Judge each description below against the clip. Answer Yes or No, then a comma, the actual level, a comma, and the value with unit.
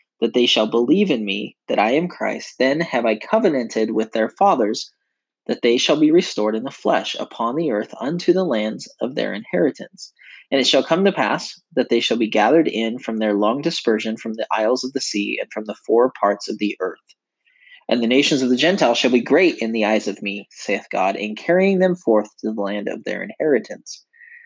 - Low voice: Yes, low, 115 Hz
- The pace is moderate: No, fast, 220 wpm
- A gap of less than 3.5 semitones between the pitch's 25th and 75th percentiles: No, average, 4.8 semitones